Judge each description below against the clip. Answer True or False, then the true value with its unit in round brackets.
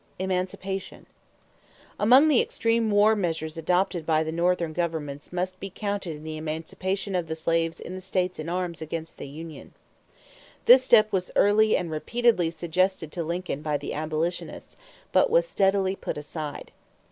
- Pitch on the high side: False (180 Hz)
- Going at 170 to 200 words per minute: False (155 wpm)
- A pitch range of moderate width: True (3.5 semitones)